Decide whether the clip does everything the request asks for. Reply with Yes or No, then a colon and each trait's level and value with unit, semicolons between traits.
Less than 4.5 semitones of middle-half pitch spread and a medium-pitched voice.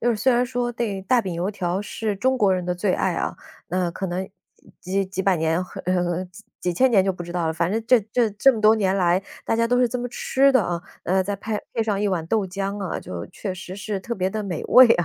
No: average, 3.8 semitones; high, 195 Hz